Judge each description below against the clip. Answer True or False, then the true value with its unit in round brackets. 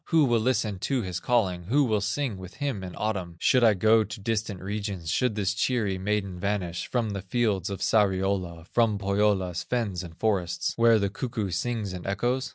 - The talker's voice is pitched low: True (105 Hz)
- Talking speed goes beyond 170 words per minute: True (190 wpm)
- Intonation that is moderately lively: True (3.6 semitones)